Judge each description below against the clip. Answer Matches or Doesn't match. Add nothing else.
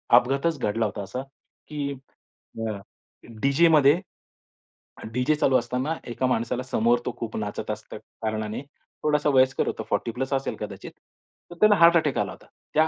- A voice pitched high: Doesn't match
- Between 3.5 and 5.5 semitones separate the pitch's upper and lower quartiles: Matches